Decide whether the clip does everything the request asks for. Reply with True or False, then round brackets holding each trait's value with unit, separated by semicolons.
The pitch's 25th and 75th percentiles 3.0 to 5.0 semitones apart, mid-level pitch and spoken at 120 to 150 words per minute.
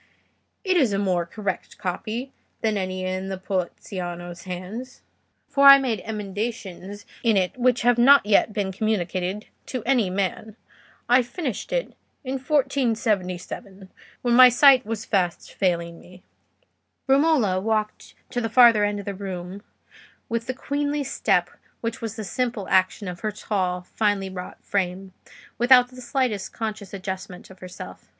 False (4.6 semitones; 210 Hz; 145 wpm)